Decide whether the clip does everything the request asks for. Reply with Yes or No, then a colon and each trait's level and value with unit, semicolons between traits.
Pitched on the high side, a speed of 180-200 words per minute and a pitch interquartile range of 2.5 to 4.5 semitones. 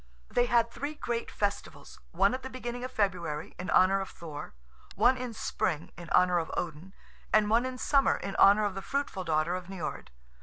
No: high, 200 Hz; average, 195 wpm; wide, 5.5 semitones